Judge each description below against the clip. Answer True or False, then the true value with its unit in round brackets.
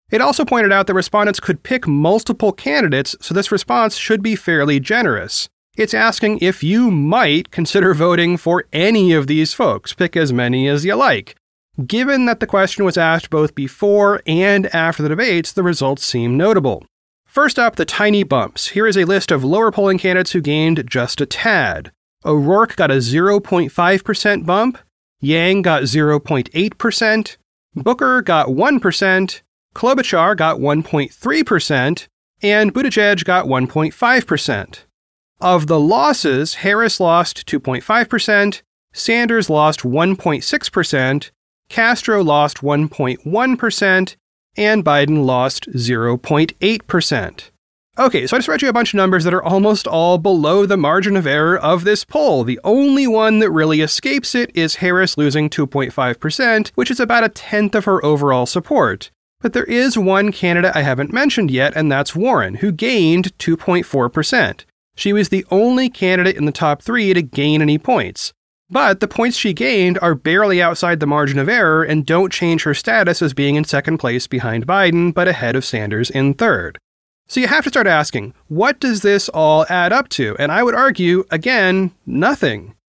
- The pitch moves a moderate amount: False (5.8 semitones)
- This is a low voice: False (180 Hz)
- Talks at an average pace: True (160 wpm)